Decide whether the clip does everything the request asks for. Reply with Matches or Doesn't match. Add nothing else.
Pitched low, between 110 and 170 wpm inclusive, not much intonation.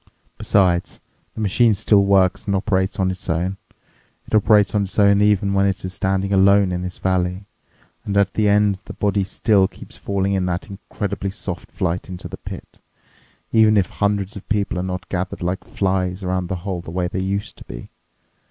Doesn't match